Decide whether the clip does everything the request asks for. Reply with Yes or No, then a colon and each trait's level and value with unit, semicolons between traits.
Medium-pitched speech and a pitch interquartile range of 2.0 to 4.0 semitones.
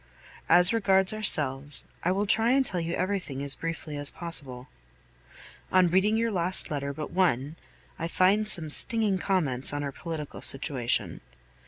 No: medium, 170 Hz; average, 5.1 semitones